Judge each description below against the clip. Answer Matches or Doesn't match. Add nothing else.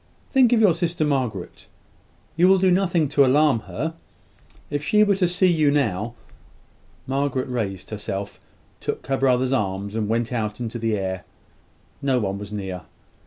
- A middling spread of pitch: Doesn't match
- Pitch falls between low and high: Doesn't match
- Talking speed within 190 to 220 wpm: Doesn't match